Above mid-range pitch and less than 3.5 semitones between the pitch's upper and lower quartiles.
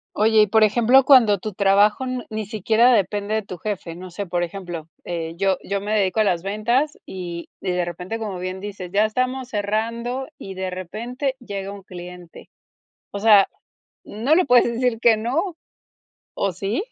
No: high, 205 Hz; average, 3.8 semitones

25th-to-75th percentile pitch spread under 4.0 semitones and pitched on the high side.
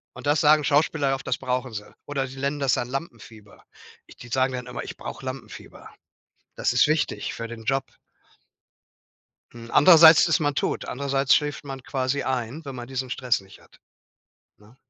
No: average, 2.8 semitones; low, 135 Hz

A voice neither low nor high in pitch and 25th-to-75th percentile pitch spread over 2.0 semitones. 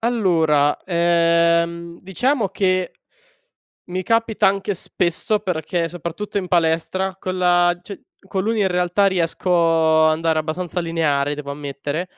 Yes: medium, 175 Hz; narrow, 2.6 semitones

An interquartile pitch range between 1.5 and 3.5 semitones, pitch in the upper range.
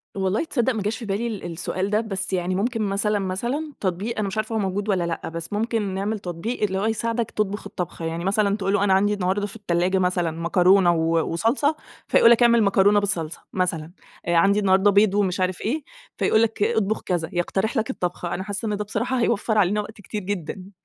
Yes: average, 2.9 semitones; high, 200 Hz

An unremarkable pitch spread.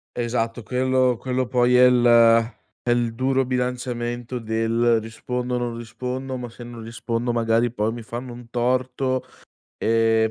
No: narrow, 1.5 semitones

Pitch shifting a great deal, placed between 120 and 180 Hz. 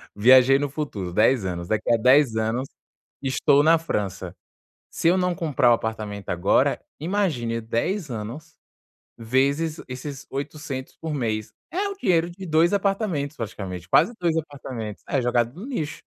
Yes: wide, 6.4 semitones; low, 135 Hz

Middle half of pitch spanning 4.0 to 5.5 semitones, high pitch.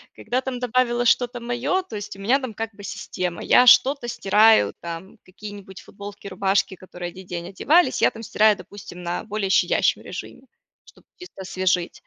Yes: average, 4.4 semitones; high, 205 Hz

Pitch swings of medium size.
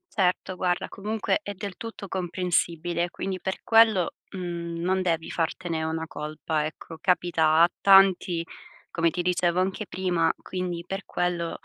No: narrow, 2.0 semitones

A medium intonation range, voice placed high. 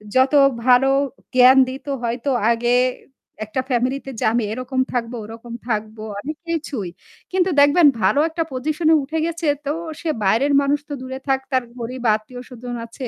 Yes: average, 3.4 semitones; very high, 255 Hz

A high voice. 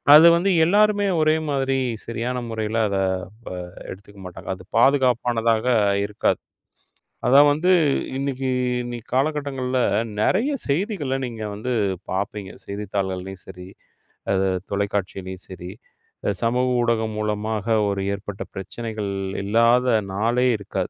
No: low, 115 Hz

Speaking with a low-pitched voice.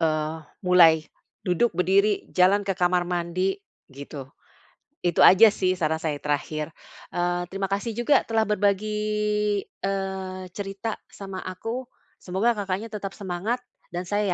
No: high, 190 Hz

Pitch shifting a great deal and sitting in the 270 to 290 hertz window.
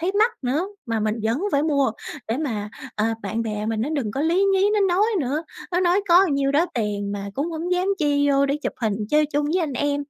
Yes: wide, 6.6 semitones; very high, 285 Hz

